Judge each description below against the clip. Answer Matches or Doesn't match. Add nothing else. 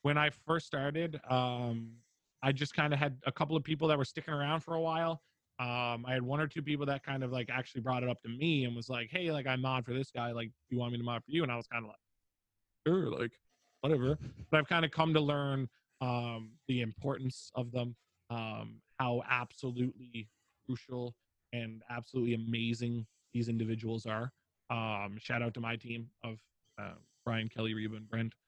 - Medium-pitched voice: Doesn't match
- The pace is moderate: Doesn't match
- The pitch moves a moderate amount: Matches